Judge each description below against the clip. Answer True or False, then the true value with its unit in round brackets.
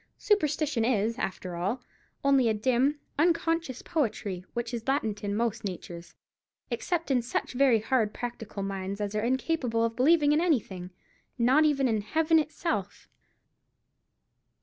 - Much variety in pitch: True (5.8 semitones)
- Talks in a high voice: True (240 Hz)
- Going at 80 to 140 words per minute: True (135 wpm)